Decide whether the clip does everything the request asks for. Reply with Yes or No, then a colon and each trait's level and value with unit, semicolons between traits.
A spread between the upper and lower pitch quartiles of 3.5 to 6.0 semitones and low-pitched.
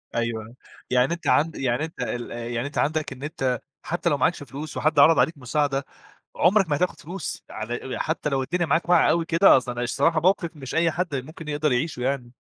No: average, 4.5 semitones; medium, 145 Hz